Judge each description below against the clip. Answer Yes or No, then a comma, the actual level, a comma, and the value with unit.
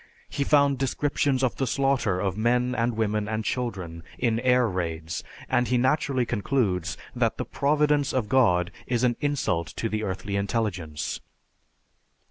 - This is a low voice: Yes, low, 115 Hz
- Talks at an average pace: Yes, average, 150 wpm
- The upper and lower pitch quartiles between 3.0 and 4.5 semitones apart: No, average, 5.2 semitones